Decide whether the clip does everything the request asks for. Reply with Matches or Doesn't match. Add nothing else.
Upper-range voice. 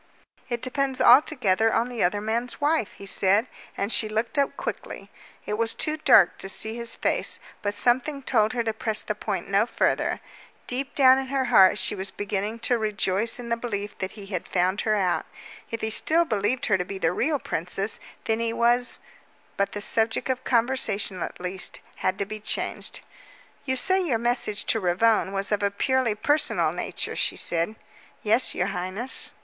Matches